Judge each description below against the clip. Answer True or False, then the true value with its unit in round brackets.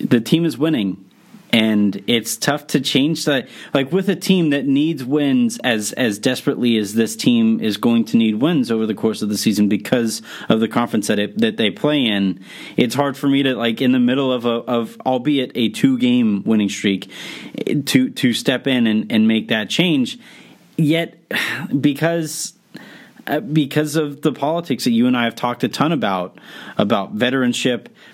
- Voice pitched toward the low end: True (130 Hz)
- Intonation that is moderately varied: False (5.7 semitones)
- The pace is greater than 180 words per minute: True (190 wpm)